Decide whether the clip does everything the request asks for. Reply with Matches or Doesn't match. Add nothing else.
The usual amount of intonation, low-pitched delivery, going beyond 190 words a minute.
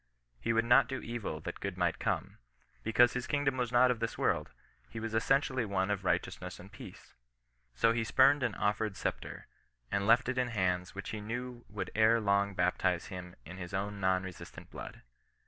Matches